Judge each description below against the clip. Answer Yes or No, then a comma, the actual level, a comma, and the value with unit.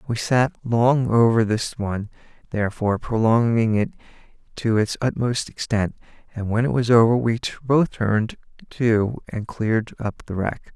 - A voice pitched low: Yes, low, 115 Hz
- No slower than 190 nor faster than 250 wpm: No, average, 150 wpm